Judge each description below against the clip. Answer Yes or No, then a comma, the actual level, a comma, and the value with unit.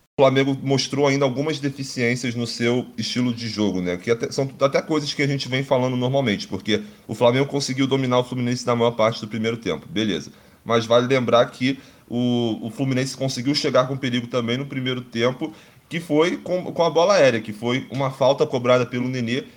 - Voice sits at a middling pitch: No, low, 125 Hz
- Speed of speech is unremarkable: No, fast, 200 wpm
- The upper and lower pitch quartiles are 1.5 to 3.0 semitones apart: Yes, narrow, 2.4 semitones